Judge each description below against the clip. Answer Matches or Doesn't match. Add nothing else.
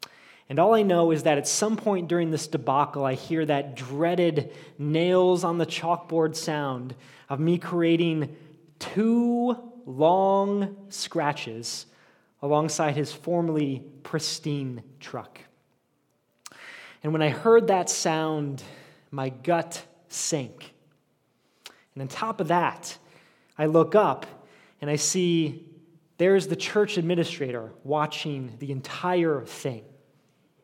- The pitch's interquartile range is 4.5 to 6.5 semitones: Doesn't match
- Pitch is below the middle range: Doesn't match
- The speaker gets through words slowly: Matches